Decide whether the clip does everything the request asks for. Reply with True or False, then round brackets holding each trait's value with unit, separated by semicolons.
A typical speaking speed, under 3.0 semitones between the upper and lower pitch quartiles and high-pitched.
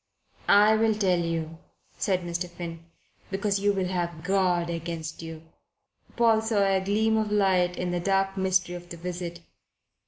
False (160 wpm; 2.6 semitones; 180 Hz)